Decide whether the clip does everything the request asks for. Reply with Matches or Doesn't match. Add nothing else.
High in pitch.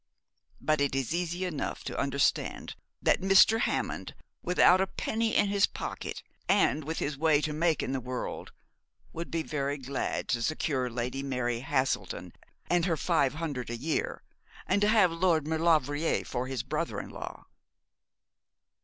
Doesn't match